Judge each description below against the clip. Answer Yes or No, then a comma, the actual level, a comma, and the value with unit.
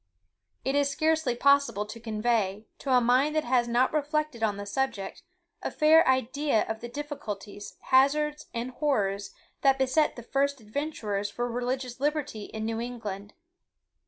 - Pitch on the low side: No, very high, 250 Hz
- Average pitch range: Yes, average, 4.4 semitones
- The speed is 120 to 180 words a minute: Yes, average, 155 wpm